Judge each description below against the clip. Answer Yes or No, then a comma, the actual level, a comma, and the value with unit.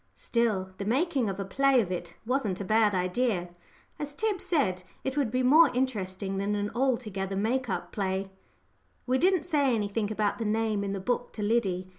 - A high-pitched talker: Yes, high, 215 Hz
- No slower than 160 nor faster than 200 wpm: Yes, average, 185 wpm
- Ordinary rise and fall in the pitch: Yes, average, 5.0 semitones